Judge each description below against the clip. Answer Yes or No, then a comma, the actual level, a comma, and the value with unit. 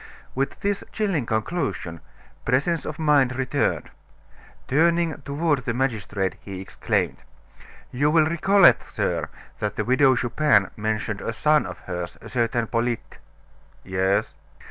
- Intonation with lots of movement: Yes, wide, 5.8 semitones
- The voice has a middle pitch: No, low, 130 Hz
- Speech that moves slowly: Yes, slow, 130 wpm